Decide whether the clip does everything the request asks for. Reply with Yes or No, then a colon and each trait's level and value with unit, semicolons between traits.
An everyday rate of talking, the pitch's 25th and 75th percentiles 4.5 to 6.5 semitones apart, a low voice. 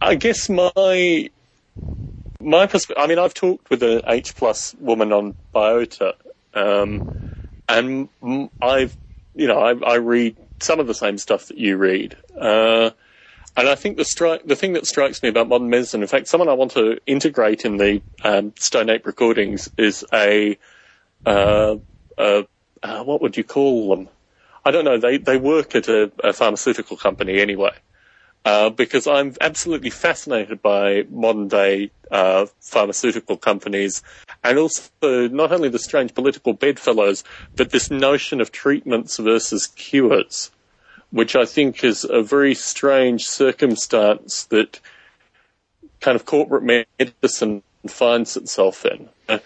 Yes: average, 150 wpm; average, 5.1 semitones; low, 115 Hz